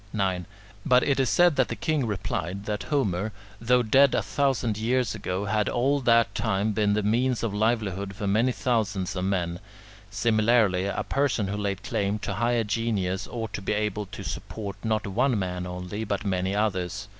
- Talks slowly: No, average, 185 wpm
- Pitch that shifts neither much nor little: Yes, average, 3.3 semitones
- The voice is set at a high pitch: No, low, 105 Hz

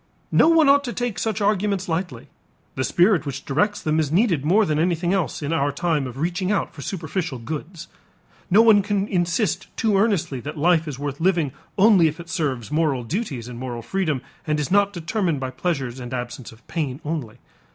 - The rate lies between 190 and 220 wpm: Yes, average, 200 wpm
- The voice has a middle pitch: Yes, medium, 165 Hz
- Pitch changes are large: Yes, wide, 5.8 semitones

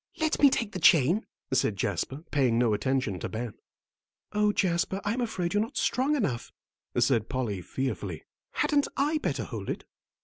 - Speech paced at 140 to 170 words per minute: Yes, average, 165 wpm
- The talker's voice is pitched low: No, medium, 160 Hz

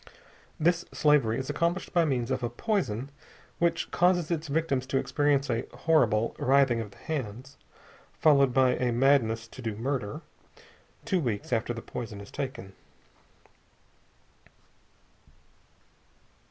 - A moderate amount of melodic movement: Yes, average, 4.6 semitones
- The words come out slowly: Yes, slow, 125 wpm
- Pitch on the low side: Yes, low, 130 Hz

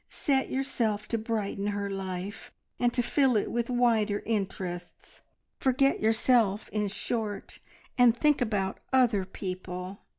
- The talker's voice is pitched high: Yes, high, 215 Hz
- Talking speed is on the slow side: Yes, slow, 130 wpm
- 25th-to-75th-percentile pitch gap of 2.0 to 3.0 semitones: No, average, 3.7 semitones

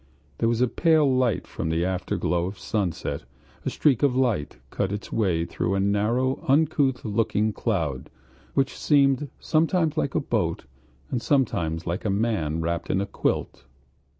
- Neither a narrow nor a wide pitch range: No, wide, 6.9 semitones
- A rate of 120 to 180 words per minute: Yes, average, 160 wpm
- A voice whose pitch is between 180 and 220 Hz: No, low, 110 Hz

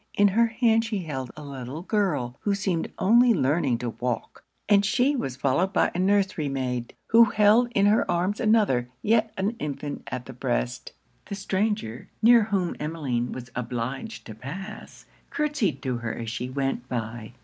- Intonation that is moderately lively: No, wide, 8.9 semitones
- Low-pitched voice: No, medium, 170 Hz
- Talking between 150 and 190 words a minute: Yes, average, 170 wpm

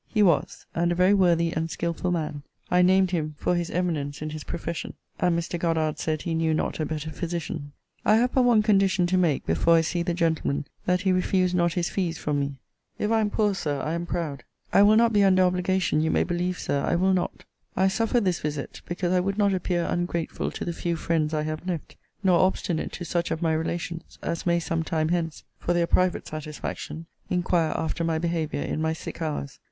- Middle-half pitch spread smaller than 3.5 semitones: Yes, narrow, 2.4 semitones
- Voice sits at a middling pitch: Yes, medium, 170 Hz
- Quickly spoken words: Yes, fast, 220 wpm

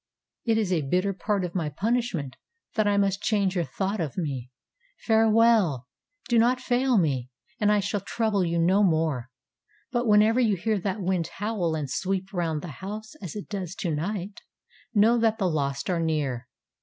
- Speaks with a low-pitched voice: No, high, 195 Hz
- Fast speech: No, average, 180 wpm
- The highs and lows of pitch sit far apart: No, average, 4.8 semitones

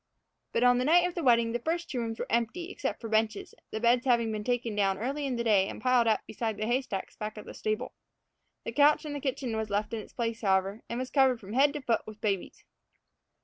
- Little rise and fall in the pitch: No, average, 3.2 semitones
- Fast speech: Yes, fast, 255 wpm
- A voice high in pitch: Yes, high, 235 Hz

